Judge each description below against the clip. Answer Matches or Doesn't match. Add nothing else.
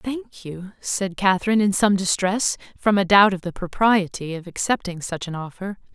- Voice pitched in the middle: Doesn't match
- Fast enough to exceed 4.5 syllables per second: Matches